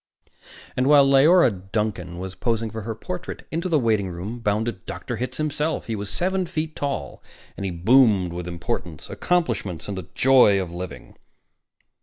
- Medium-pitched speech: No, low, 110 Hz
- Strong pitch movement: Yes, wide, 6.9 semitones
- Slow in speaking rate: No, average, 160 wpm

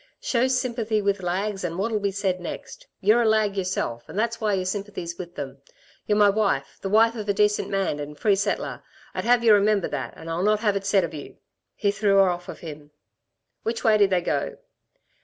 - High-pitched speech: Yes, high, 200 Hz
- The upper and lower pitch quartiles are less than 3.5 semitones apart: Yes, average, 3.0 semitones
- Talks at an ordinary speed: No, fast, 220 wpm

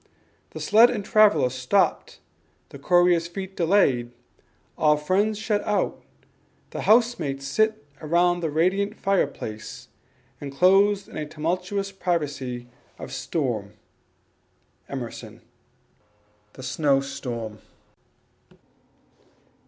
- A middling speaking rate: No, slow, 95 wpm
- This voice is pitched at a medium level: Yes, medium, 170 Hz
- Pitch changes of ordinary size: No, wide, 6.4 semitones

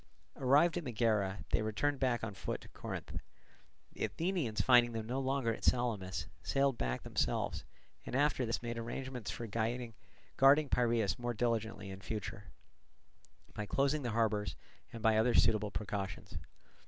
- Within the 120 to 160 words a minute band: Yes, average, 150 wpm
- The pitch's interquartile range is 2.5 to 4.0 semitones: Yes, average, 3.3 semitones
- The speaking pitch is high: No, low, 115 Hz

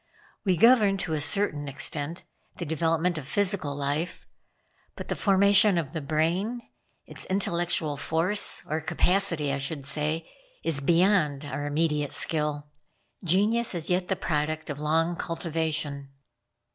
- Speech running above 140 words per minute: No, slow, 135 wpm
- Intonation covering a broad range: No, average, 3.8 semitones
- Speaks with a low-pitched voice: No, medium, 160 Hz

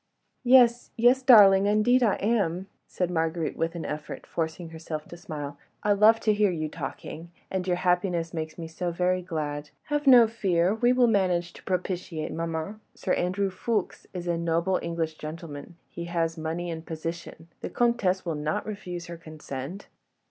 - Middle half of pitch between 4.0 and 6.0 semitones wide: No, average, 3.6 semitones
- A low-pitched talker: No, medium, 175 Hz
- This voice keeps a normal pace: Yes, average, 170 wpm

